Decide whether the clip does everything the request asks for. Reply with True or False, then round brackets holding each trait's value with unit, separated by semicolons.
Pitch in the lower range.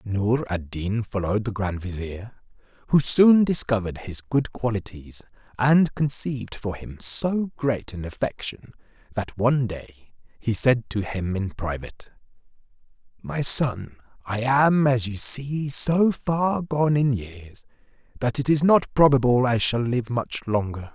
True (120 Hz)